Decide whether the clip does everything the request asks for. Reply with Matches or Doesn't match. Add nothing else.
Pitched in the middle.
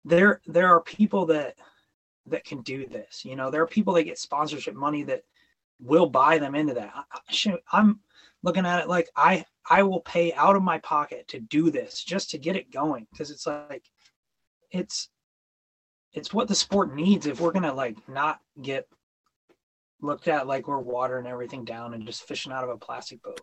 Matches